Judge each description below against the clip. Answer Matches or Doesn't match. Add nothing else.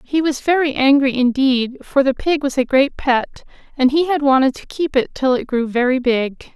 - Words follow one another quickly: Matches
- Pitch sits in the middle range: Doesn't match